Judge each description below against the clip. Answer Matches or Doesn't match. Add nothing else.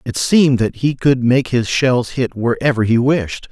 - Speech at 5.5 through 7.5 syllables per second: Doesn't match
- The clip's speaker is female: Doesn't match